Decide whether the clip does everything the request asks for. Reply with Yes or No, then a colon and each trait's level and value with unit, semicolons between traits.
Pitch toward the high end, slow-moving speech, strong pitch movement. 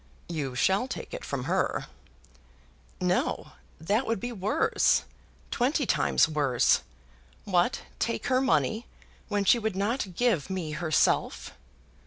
Yes: high, 200 Hz; slow, 125 wpm; wide, 6.6 semitones